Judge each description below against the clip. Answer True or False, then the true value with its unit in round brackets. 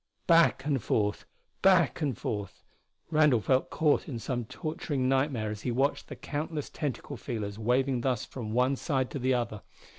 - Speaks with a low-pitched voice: True (130 Hz)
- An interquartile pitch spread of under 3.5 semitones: False (3.9 semitones)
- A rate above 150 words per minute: True (170 wpm)